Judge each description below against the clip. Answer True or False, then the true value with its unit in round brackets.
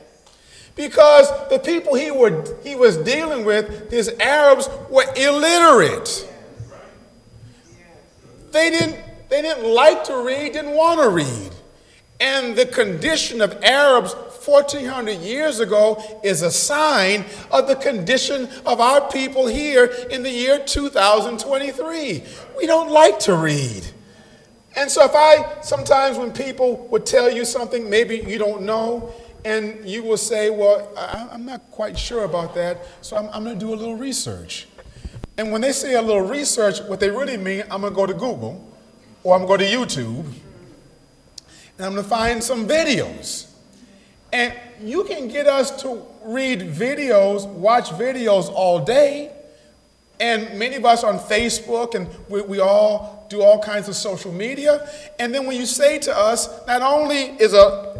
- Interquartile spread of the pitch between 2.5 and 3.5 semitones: False (5.2 semitones)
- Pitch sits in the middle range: False (240 Hz)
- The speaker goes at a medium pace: True (160 wpm)